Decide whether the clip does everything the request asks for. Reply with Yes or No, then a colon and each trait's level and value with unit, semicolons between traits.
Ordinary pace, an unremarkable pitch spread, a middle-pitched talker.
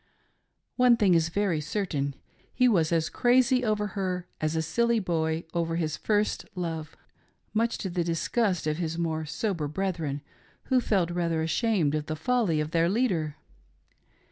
Yes: average, 165 wpm; average, 4.9 semitones; medium, 170 Hz